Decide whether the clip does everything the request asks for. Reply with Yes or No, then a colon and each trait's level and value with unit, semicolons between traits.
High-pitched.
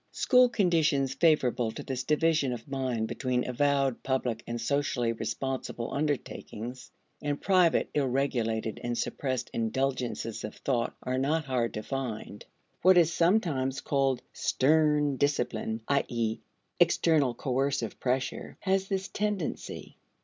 No: low, 135 Hz